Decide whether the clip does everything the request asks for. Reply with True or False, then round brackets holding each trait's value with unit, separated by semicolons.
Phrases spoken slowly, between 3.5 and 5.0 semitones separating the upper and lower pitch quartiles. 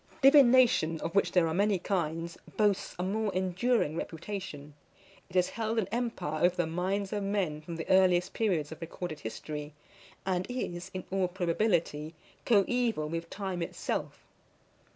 False (150 wpm; 3.9 semitones)